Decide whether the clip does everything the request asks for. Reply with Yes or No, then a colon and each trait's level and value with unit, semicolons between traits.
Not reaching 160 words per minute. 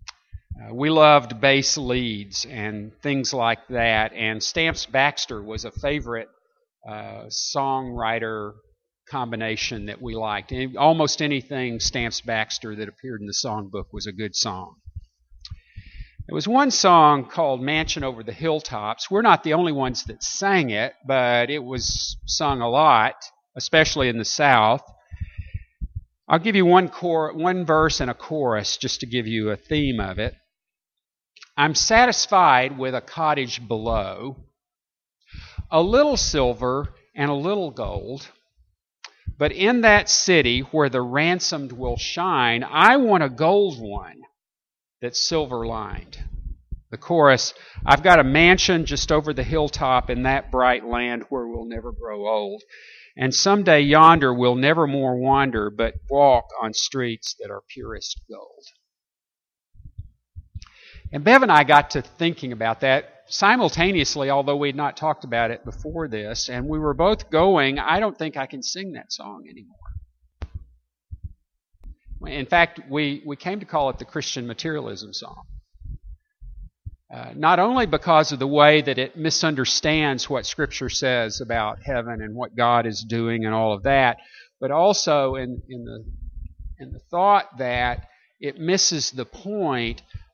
Yes: average, 150 wpm